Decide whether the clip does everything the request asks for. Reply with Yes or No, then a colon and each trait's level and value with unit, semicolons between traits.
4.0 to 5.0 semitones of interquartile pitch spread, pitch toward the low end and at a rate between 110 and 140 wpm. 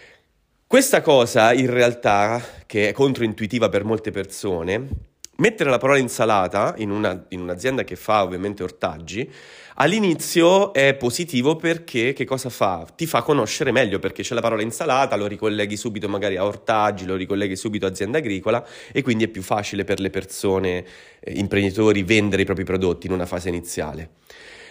No: average, 4.3 semitones; low, 105 Hz; average, 165 wpm